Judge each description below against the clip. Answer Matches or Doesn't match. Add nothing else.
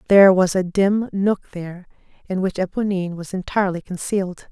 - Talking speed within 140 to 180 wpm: Matches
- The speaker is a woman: Matches